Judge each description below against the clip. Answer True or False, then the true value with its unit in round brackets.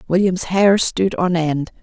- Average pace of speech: True (165 wpm)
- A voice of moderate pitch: True (180 Hz)